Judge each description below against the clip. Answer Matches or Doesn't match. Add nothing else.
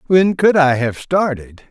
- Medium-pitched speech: Matches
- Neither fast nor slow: Matches